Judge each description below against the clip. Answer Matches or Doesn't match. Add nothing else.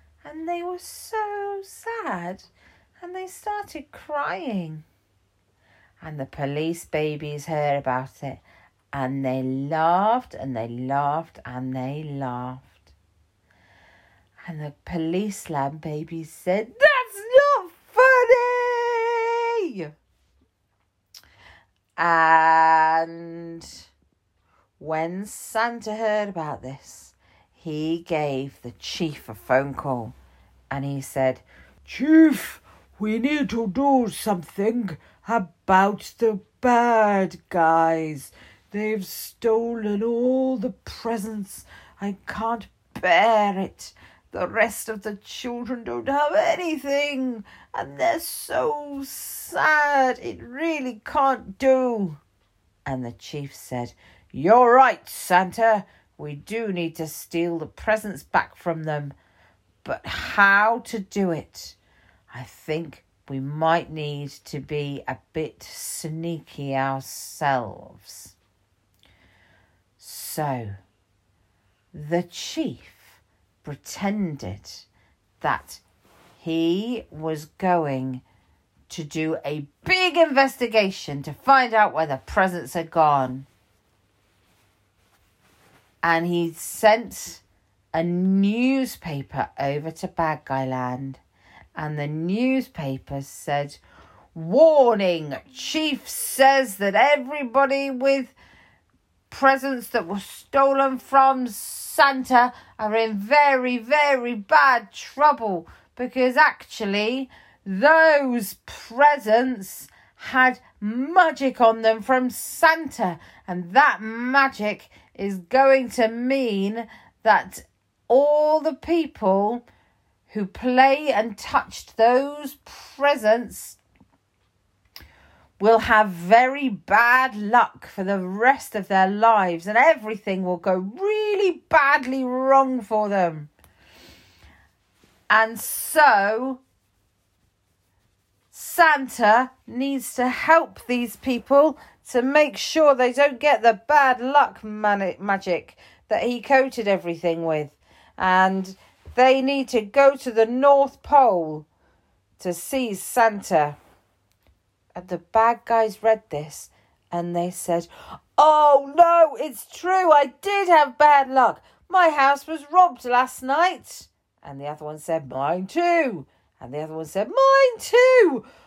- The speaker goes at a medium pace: Doesn't match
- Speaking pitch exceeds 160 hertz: Matches